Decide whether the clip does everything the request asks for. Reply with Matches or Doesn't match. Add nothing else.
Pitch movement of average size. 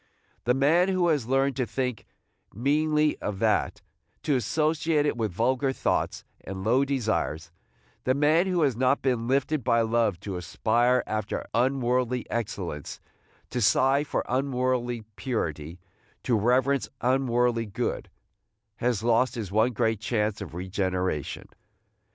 Matches